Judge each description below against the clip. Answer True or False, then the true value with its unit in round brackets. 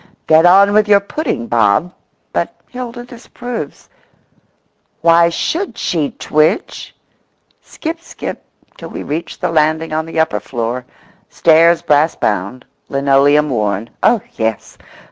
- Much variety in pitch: True (6.9 semitones)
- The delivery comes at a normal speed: False (125 wpm)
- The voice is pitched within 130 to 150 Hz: False (160 Hz)